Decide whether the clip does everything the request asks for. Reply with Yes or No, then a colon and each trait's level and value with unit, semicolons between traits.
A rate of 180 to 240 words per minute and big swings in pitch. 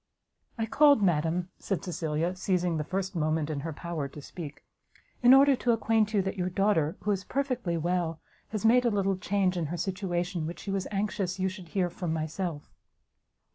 No: average, 190 wpm; average, 3.6 semitones